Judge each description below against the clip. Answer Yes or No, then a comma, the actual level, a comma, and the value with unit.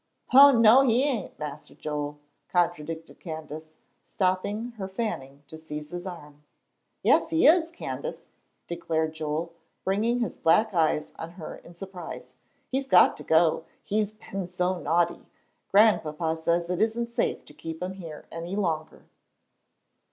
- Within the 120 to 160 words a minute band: Yes, average, 145 wpm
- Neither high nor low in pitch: Yes, medium, 175 Hz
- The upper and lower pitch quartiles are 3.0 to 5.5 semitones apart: Yes, average, 5.1 semitones